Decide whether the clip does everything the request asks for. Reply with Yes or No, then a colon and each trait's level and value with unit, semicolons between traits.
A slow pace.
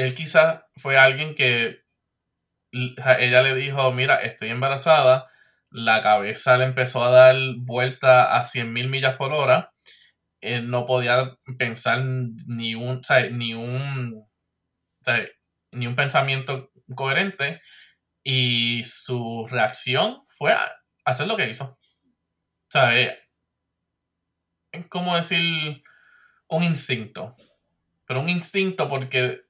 Yes: slow, 120 wpm